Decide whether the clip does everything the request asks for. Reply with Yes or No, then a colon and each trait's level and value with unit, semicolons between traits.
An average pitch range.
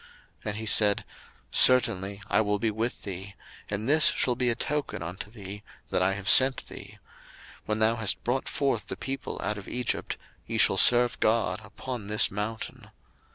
Yes: average, 3.2 semitones